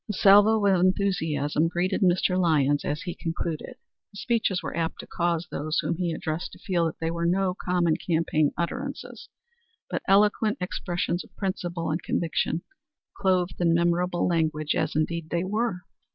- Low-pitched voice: No, medium, 175 Hz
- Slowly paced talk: No, average, 165 wpm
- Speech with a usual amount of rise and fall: No, narrow, 2.3 semitones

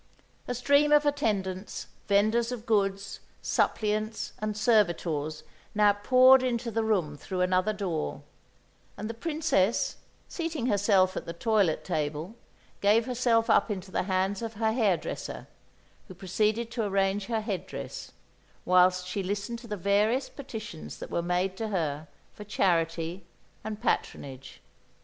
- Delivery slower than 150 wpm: Yes, average, 140 wpm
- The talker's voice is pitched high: Yes, high, 205 Hz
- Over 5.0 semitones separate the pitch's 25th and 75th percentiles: No, average, 3.6 semitones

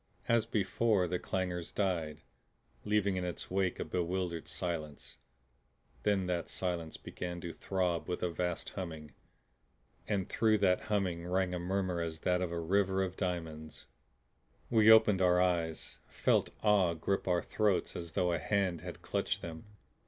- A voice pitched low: Yes, very low, 90 Hz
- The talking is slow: No, average, 155 wpm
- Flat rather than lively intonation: Yes, narrow, 2.3 semitones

